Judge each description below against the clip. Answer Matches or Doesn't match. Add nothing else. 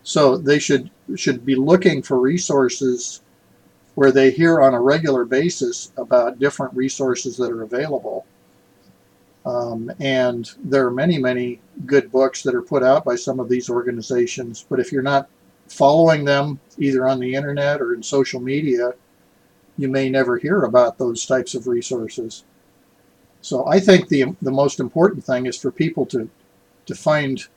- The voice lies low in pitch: Matches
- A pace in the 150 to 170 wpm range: Matches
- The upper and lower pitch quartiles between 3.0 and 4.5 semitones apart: Doesn't match